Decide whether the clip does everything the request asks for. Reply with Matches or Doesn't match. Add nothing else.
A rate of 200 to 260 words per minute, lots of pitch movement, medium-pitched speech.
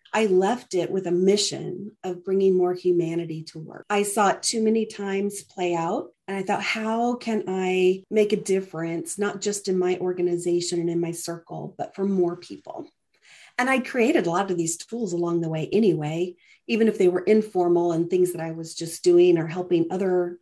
Doesn't match